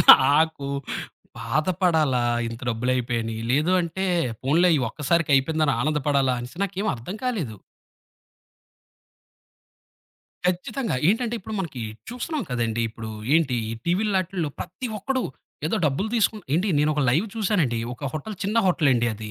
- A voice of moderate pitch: Yes, medium, 155 Hz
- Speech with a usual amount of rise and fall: No, wide, 6.7 semitones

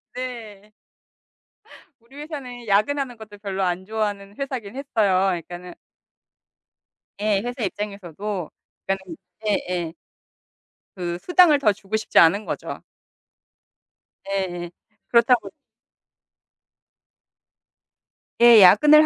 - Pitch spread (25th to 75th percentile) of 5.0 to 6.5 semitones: No, average, 4.4 semitones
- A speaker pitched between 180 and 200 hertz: No, high, 210 Hz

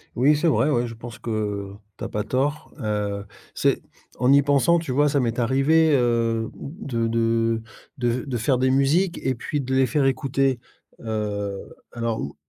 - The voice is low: Yes, low, 125 Hz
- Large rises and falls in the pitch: No, average, 3.4 semitones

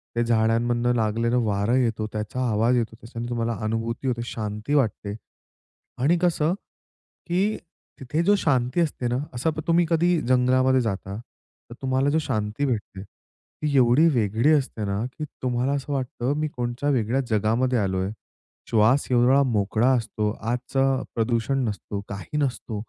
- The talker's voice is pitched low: Yes, low, 120 Hz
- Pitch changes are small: No, average, 3.5 semitones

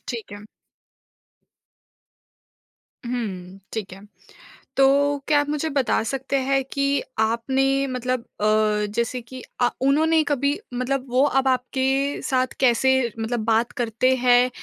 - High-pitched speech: Yes, very high, 255 Hz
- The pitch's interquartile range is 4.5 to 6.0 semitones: No, average, 2.9 semitones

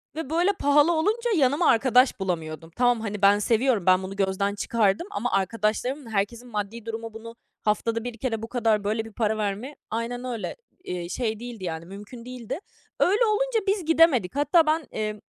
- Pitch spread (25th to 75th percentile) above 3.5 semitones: Yes, average, 4.6 semitones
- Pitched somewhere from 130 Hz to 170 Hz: No, high, 230 Hz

